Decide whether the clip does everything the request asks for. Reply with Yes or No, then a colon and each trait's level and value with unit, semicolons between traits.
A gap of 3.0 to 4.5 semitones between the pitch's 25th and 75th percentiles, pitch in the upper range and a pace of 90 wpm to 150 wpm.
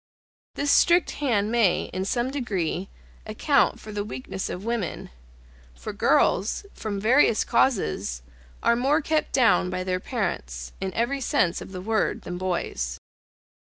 No: average, 5.0 semitones; high, 205 Hz; average, 145 wpm